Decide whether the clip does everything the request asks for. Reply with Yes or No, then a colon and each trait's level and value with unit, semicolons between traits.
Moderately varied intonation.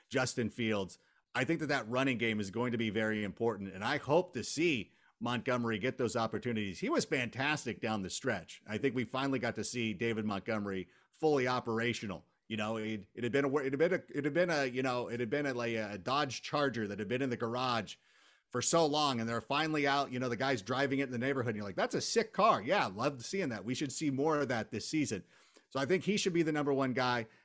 Yes: average, 3.8 semitones